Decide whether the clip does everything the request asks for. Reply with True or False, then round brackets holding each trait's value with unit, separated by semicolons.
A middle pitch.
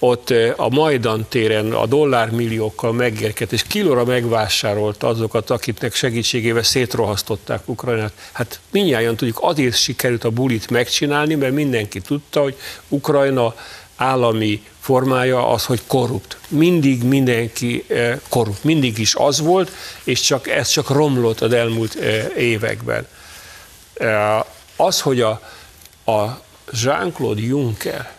False (120 Hz)